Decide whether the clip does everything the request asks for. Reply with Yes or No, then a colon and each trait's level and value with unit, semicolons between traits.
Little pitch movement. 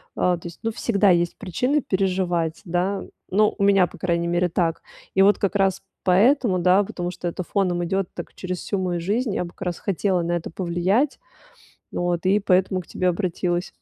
Yes: narrow, 2.2 semitones